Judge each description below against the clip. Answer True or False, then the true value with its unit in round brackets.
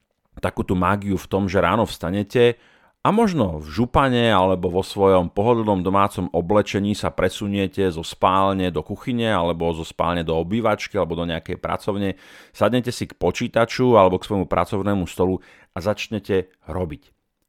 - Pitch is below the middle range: True (95 Hz)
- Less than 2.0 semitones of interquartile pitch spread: False (2.8 semitones)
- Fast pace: False (150 wpm)